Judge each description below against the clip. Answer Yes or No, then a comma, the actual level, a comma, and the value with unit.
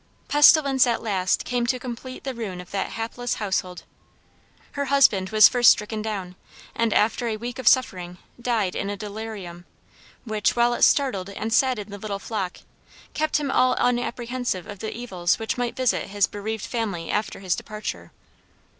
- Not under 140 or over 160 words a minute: No, average, 170 wpm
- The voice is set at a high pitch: Yes, high, 220 Hz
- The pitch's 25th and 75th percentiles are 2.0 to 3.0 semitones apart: No, average, 3.7 semitones